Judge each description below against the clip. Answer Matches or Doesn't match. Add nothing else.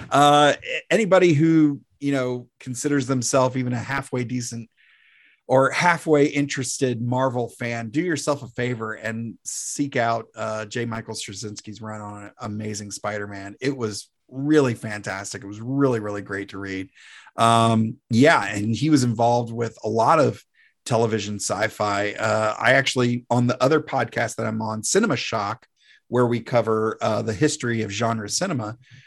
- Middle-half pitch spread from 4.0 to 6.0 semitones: Doesn't match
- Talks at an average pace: Matches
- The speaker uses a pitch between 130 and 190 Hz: Doesn't match